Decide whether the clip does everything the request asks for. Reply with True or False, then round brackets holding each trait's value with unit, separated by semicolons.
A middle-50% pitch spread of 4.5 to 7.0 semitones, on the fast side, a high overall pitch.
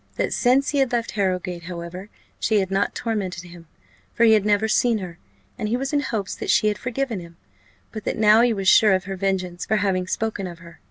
False (3.5 semitones; 230 wpm; 205 Hz)